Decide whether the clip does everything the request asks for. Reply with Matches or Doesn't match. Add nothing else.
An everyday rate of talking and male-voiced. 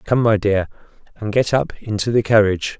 Matches